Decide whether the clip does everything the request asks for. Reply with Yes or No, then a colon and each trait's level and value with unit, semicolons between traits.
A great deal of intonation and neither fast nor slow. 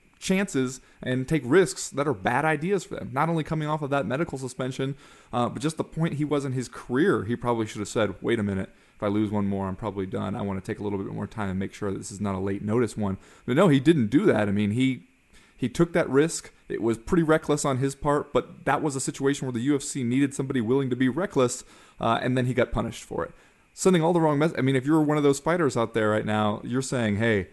No: wide, 5.7 semitones; fast, 275 wpm